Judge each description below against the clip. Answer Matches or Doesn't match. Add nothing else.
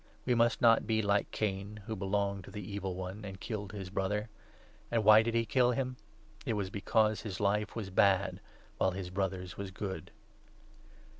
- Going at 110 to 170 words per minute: Doesn't match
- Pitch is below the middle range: Matches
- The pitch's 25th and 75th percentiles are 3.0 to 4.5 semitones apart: Doesn't match